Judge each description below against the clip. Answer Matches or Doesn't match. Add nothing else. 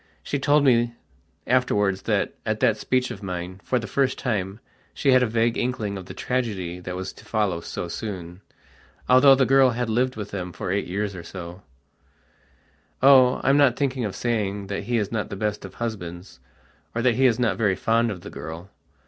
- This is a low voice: Matches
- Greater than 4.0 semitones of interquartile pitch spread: Matches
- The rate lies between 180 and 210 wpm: Matches